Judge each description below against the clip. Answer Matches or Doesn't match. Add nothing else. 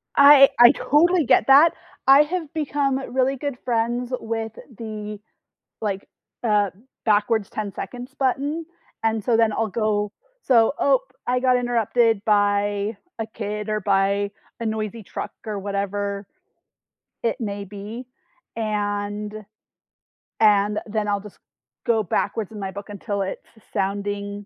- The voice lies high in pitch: Matches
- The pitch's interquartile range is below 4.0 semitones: Matches